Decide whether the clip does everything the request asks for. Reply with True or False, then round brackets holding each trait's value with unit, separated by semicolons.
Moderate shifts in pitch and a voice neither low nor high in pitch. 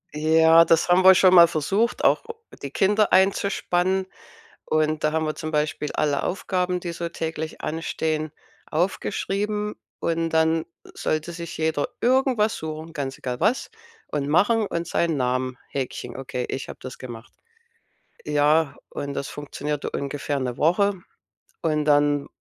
True (3.6 semitones; 160 Hz)